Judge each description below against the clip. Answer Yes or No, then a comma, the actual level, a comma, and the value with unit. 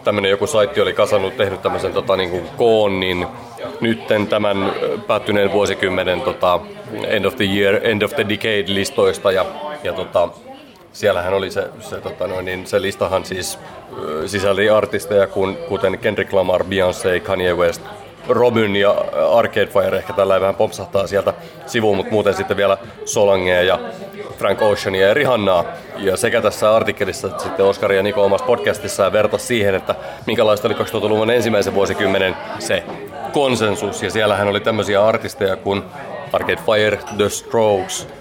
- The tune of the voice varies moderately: No, narrow, 2.1 semitones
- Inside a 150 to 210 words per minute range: Yes, fast, 155 wpm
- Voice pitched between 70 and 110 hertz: Yes, low, 100 Hz